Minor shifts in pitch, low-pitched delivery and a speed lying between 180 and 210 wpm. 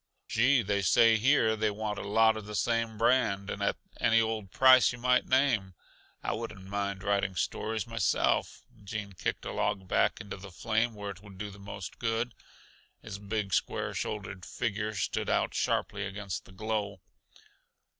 No: narrow, 2.3 semitones; low, 105 Hz; average, 170 wpm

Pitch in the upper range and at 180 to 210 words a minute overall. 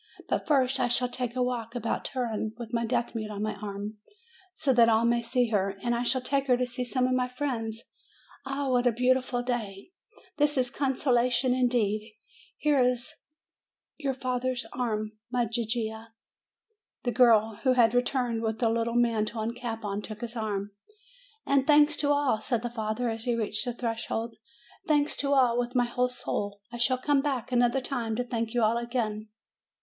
Yes: high, 240 Hz; average, 185 wpm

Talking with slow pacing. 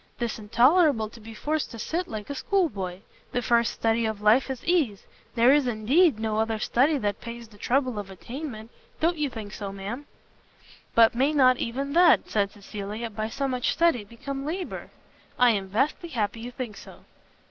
No: average, 190 wpm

